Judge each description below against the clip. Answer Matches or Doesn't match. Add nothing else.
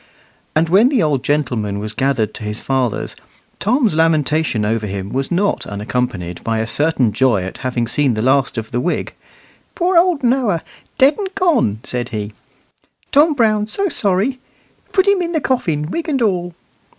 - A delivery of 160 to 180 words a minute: Matches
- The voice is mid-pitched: Matches